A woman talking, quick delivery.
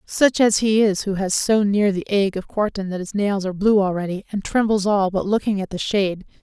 Yes: female; fast, 245 wpm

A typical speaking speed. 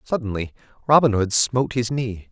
Yes: average, 155 wpm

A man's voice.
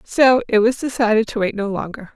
No: female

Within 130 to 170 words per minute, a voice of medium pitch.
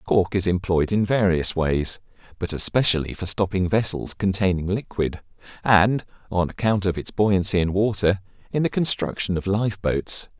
No: average, 155 wpm; very low, 95 Hz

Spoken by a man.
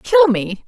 No: female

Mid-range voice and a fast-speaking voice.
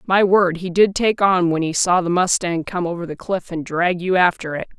Yes: medium, 180 Hz; fast, 250 wpm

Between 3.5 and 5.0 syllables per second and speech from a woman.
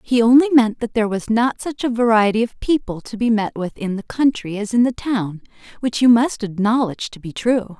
No: 5.3 syllables/s; female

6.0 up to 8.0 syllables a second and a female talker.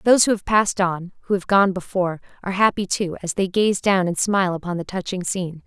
Yes: 6.3 syllables/s; female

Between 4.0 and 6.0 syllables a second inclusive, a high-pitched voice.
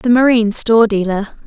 Yes: 5.9 syllables/s; high, 225 Hz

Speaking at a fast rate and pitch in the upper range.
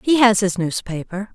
No: average, 180 wpm; high, 205 Hz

